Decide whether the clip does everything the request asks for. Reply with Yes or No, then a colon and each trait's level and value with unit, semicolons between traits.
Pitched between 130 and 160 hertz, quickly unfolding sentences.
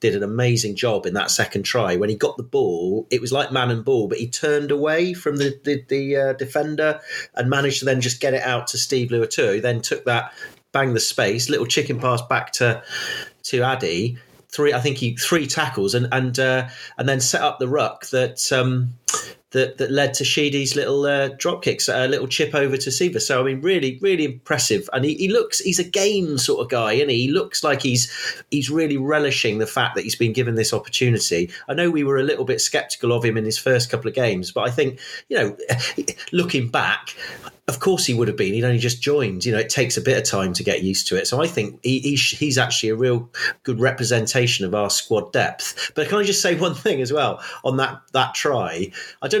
Yes: low, 135 Hz; fast, 235 wpm